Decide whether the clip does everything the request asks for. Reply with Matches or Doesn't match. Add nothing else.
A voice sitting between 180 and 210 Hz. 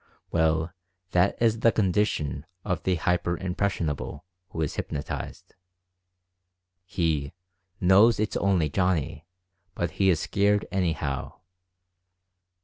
Doesn't match